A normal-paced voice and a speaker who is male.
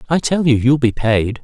No: fast, 250 wpm; male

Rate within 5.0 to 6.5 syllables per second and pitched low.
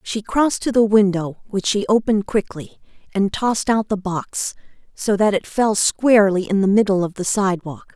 No: 5.2 syllables/s; high, 205 Hz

